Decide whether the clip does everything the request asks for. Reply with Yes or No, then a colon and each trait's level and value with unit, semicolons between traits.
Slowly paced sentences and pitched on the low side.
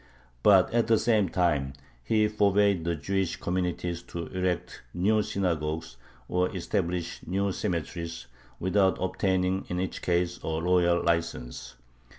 Yes: slow, 130 wpm; very low, 90 Hz